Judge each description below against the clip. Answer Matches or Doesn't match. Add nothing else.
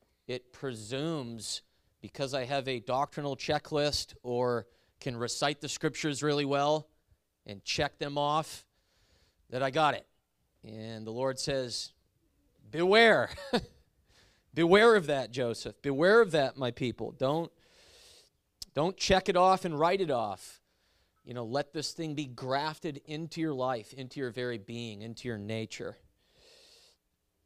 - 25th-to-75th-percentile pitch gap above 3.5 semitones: Matches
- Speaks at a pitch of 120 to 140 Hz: Matches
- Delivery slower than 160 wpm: Matches